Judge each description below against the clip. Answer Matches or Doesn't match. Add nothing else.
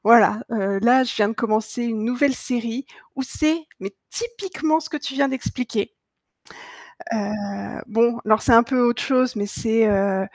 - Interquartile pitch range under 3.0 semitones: Doesn't match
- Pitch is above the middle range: Matches